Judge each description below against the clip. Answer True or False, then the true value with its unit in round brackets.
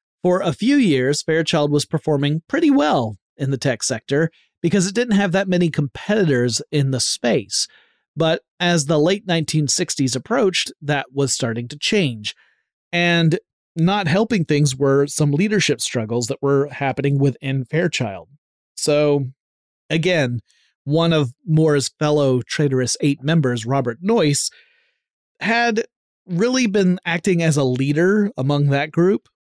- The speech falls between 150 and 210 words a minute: False (140 wpm)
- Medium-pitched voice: True (150 Hz)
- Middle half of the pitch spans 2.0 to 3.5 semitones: False (4.3 semitones)